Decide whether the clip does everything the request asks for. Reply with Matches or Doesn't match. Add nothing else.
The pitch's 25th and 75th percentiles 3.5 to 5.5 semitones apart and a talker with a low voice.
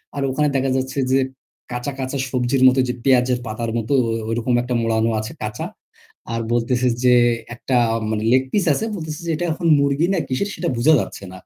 Doesn't match